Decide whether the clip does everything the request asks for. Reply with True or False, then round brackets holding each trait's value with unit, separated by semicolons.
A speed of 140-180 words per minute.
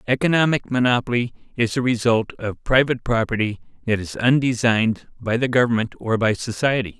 True (145 wpm)